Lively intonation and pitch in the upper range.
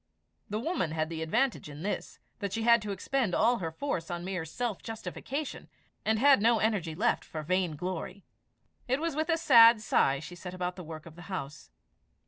Yes: wide, 6.1 semitones; high, 195 Hz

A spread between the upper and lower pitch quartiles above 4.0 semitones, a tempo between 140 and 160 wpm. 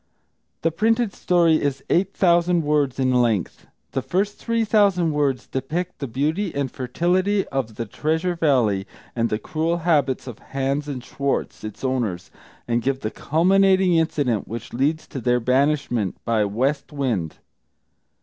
Yes: wide, 5.6 semitones; average, 150 wpm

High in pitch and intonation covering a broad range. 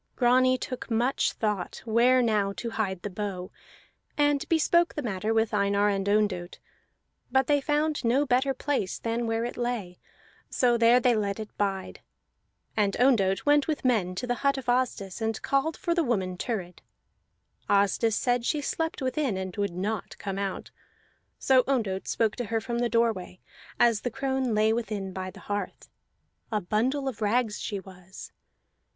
No: high, 230 Hz; average, 4.3 semitones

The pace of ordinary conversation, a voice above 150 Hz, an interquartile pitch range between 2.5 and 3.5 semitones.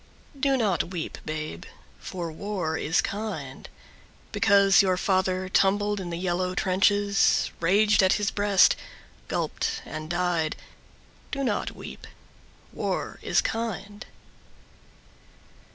No: slow, 110 wpm; high, 190 Hz; average, 2.8 semitones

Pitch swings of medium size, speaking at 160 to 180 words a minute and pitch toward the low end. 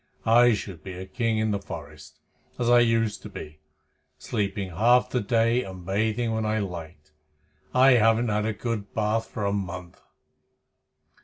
Yes: average, 3.0 semitones; average, 165 wpm; low, 110 Hz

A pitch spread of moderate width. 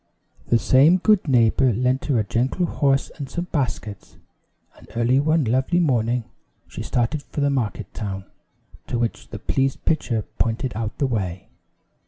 Yes: average, 3.7 semitones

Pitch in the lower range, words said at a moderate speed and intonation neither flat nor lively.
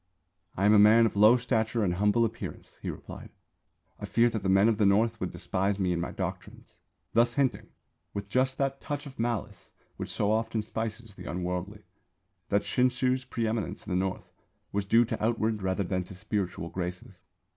Yes: low, 105 Hz; average, 190 wpm; average, 3.2 semitones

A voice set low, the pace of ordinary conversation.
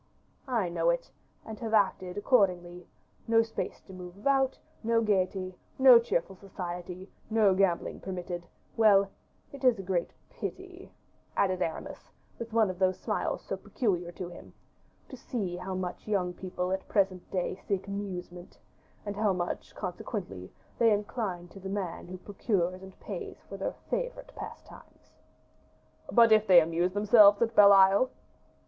No: high, 195 Hz; average, 155 wpm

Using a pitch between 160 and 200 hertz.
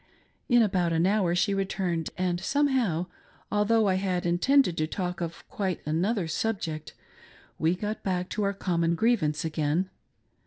Yes: medium, 185 Hz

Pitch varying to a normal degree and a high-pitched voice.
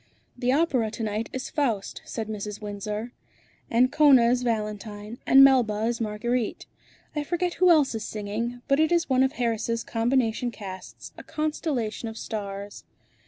Yes: average, 3.8 semitones; high, 235 Hz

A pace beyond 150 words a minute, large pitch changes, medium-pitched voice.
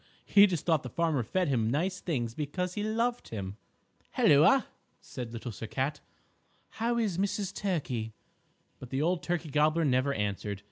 Yes: average, 160 wpm; wide, 7.2 semitones; medium, 150 Hz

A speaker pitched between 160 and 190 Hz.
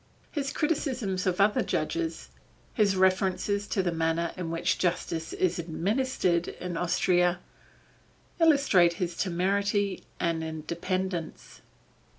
Yes: medium, 185 Hz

